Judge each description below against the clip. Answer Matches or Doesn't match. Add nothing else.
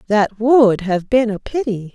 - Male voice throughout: Doesn't match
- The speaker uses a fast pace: Doesn't match